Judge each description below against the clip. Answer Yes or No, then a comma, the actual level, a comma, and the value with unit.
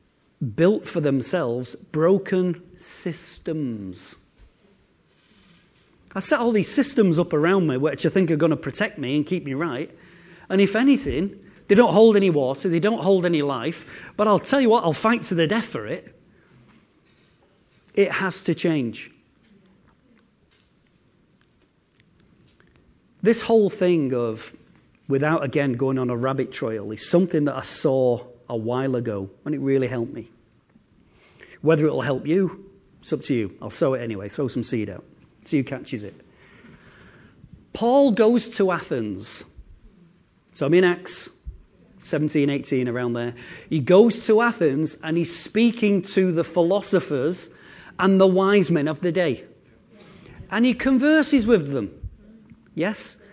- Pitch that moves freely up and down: Yes, wide, 6.5 semitones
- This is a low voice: No, medium, 170 Hz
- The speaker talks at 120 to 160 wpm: Yes, average, 150 wpm